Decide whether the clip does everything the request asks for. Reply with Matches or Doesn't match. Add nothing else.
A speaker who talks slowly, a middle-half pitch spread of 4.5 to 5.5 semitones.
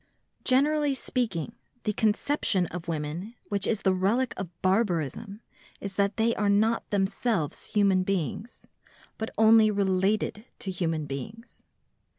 Doesn't match